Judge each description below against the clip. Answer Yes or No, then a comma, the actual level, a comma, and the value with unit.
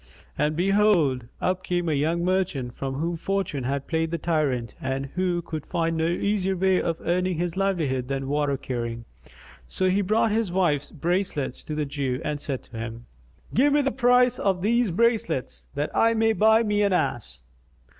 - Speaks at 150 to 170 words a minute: No, average, 185 wpm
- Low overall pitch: No, medium, 170 Hz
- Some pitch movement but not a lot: No, wide, 5.8 semitones